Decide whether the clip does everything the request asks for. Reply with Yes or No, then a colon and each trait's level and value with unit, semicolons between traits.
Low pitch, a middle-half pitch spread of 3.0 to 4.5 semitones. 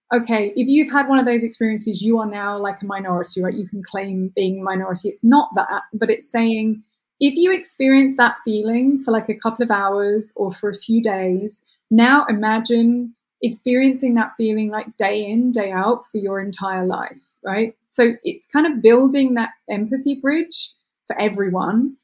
No: high, 225 Hz; average, 3.5 semitones